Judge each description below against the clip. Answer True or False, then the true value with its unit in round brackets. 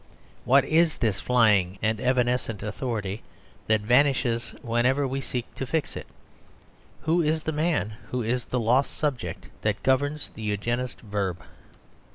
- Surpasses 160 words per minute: False (145 wpm)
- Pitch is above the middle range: False (125 Hz)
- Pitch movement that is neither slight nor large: True (4.1 semitones)